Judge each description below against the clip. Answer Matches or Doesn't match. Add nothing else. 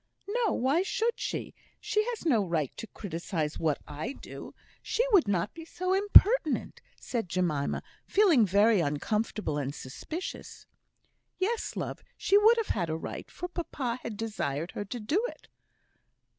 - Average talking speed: Matches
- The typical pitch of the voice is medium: Doesn't match